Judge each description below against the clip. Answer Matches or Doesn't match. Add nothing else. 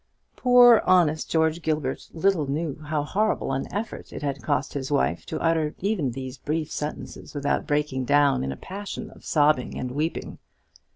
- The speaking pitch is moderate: Matches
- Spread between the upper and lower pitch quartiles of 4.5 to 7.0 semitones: Doesn't match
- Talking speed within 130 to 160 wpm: Doesn't match